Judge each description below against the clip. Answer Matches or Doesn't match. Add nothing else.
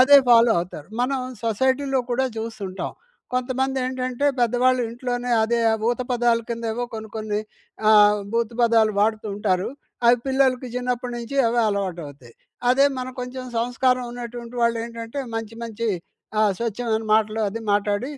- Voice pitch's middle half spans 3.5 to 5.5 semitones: Doesn't match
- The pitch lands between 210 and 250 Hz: Matches